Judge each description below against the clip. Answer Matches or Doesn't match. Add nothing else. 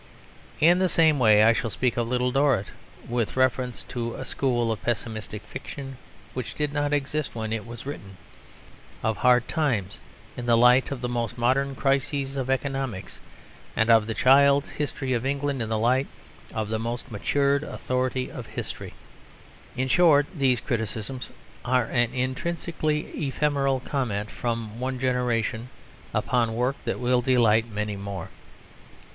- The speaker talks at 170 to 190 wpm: Doesn't match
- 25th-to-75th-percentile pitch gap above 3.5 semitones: Doesn't match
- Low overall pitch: Matches